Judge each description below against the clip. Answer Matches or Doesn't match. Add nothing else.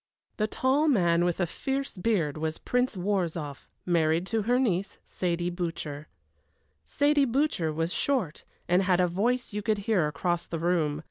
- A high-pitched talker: Doesn't match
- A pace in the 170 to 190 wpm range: Doesn't match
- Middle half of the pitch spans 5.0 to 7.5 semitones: Matches